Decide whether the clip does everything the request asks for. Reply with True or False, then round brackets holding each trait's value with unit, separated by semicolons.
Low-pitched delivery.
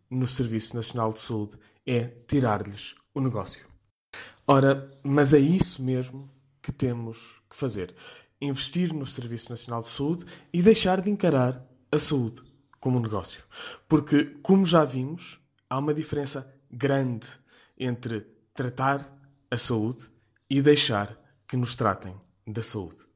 True (130 Hz)